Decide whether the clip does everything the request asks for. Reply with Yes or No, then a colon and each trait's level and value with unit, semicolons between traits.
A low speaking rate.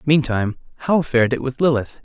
No: average, 175 wpm